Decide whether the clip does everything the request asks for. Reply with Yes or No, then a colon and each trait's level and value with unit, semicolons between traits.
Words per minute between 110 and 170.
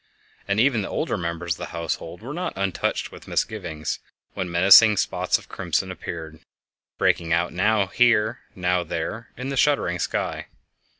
Yes: average, 160 wpm